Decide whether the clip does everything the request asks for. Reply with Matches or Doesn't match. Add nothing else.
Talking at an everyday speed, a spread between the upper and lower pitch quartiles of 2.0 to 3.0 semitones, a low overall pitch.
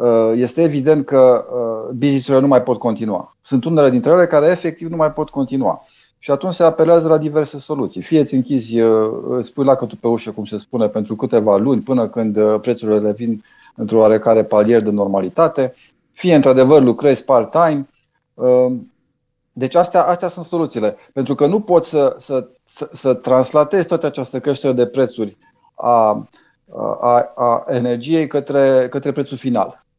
Doesn't match